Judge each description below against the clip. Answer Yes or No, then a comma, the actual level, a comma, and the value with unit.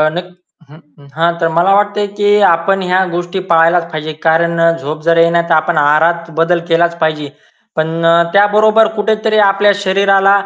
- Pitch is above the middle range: No, medium, 170 Hz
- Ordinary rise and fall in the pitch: Yes, average, 3.2 semitones